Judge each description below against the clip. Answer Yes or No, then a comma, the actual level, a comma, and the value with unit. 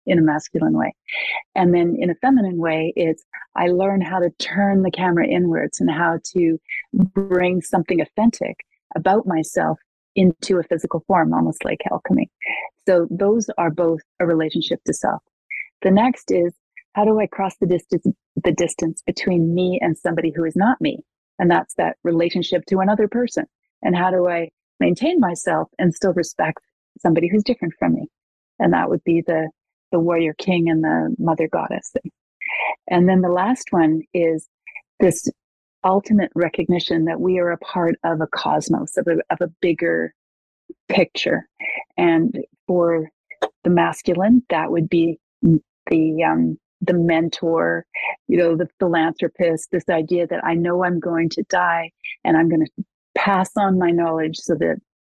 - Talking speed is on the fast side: No, average, 165 wpm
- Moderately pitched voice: Yes, medium, 175 Hz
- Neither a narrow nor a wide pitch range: No, narrow, 2.3 semitones